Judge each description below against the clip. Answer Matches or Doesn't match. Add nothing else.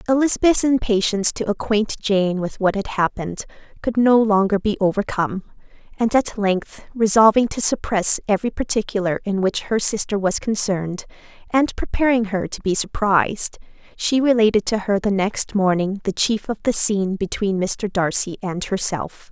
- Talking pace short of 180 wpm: Matches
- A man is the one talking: Doesn't match